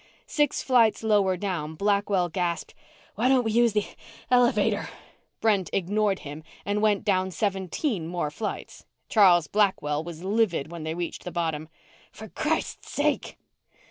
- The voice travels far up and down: No, average, 4.0 semitones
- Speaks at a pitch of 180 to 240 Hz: Yes, high, 190 Hz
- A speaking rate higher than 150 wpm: No, average, 145 wpm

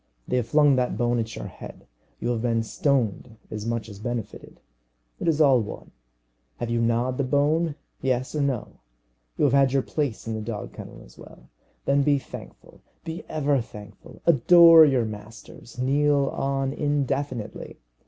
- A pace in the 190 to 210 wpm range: No, average, 170 wpm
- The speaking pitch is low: Yes, low, 130 Hz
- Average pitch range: Yes, average, 3.8 semitones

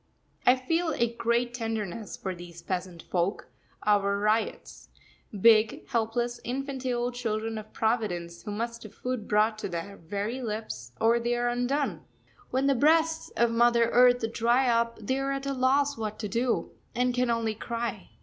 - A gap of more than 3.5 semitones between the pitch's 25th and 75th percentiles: No, average, 2.8 semitones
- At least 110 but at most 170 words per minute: Yes, average, 165 wpm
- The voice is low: No, high, 230 Hz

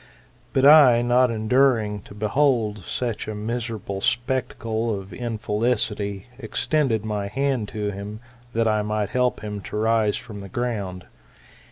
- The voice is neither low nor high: No, low, 110 Hz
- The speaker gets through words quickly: No, average, 140 wpm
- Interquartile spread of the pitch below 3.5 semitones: Yes, average, 2.9 semitones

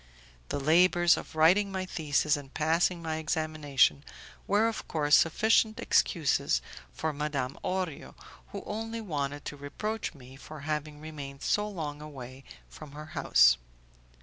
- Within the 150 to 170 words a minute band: No, average, 140 wpm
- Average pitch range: Yes, average, 3.7 semitones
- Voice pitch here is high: No, medium, 155 Hz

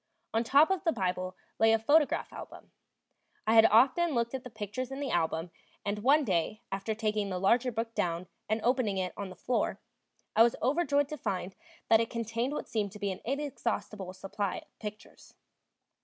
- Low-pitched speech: No, high, 225 Hz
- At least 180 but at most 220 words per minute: Yes, average, 190 wpm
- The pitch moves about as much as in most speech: Yes, average, 4.5 semitones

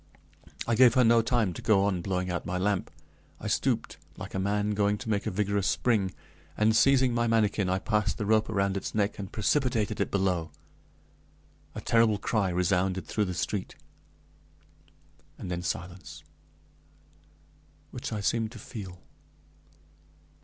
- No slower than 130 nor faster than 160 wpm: Yes, average, 155 wpm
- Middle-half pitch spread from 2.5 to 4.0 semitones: Yes, average, 2.9 semitones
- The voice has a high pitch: No, low, 100 Hz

